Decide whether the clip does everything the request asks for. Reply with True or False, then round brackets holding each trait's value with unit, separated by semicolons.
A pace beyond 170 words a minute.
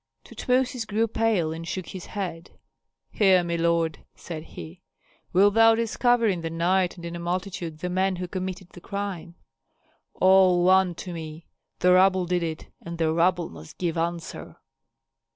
False (165 wpm)